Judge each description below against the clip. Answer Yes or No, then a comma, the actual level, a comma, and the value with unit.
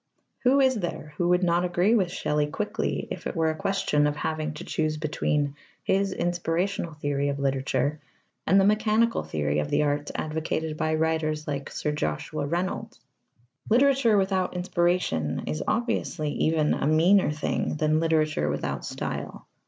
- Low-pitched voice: No, medium, 160 Hz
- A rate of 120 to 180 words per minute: Yes, average, 160 wpm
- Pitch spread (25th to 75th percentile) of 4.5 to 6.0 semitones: No, average, 3.8 semitones